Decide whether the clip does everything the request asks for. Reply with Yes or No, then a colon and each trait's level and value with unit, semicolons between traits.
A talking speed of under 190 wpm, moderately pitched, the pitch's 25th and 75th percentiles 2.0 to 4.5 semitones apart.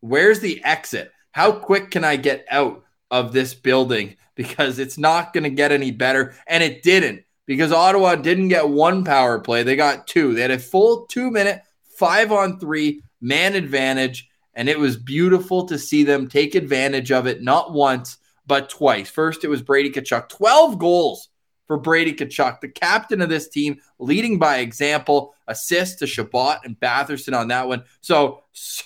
No: average, 180 wpm; medium, 145 Hz; average, 4.9 semitones